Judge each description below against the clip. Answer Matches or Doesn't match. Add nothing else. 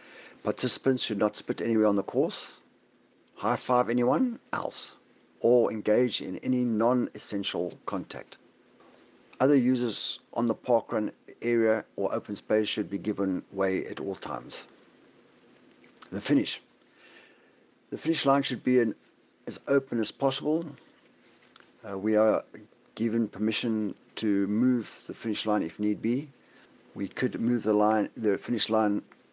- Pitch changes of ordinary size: Matches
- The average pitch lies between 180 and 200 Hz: Doesn't match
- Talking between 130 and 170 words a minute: Matches